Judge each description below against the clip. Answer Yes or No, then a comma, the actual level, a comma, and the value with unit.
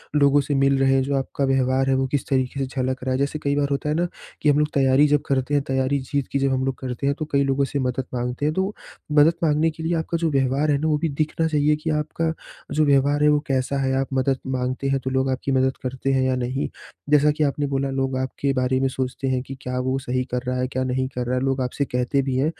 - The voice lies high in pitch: No, low, 135 Hz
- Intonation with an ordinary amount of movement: No, narrow, 1.8 semitones